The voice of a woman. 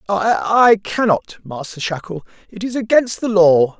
No: male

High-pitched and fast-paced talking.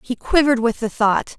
Yes: high, 240 Hz; fast, 215 wpm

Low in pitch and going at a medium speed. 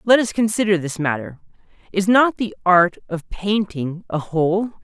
No: high, 190 Hz; average, 160 wpm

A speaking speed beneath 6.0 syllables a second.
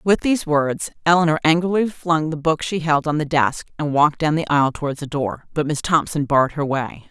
Yes: 5.5 syllables/s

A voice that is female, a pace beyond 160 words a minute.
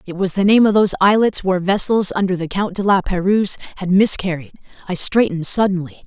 Yes: female; average, 200 wpm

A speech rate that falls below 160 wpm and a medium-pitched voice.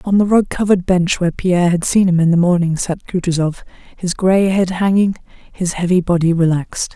No: average, 200 wpm; medium, 180 Hz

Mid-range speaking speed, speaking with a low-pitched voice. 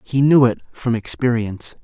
Yes: average, 165 wpm; low, 120 Hz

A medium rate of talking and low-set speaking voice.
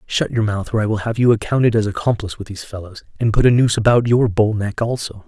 No: fast, 260 wpm; low, 110 Hz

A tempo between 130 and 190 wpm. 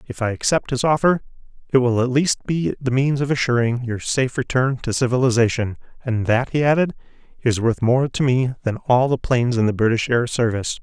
No: fast, 205 wpm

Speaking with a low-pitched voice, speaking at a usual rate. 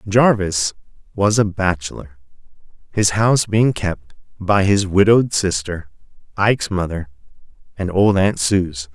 No: very low, 95 Hz; slow, 120 wpm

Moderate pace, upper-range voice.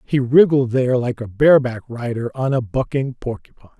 No: average, 175 wpm; low, 125 Hz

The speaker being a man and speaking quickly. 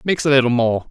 Yes: male; fast, 265 wpm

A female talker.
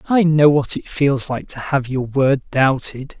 No: male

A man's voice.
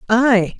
No: female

